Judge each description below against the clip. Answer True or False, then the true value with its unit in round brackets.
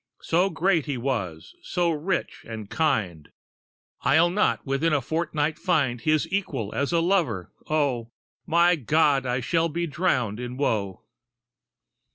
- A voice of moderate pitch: True (150 Hz)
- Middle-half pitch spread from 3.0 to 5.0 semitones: False (5.5 semitones)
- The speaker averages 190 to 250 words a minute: False (140 wpm)